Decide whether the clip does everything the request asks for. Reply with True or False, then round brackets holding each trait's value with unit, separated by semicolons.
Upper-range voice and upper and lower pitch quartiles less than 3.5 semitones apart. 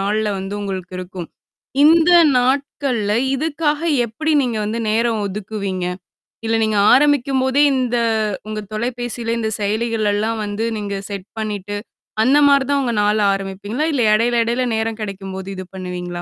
False (220 Hz; 3.9 semitones)